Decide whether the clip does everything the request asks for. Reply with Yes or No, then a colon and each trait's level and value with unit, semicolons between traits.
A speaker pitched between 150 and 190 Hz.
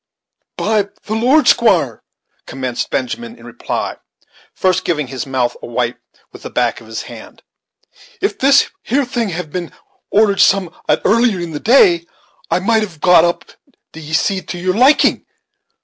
Yes: medium, 185 Hz